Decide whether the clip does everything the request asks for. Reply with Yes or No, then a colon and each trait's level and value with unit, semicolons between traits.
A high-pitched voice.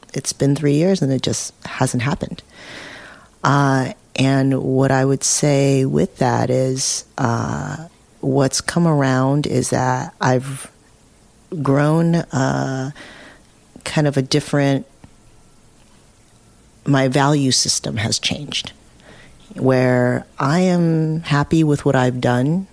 No: low, 135 Hz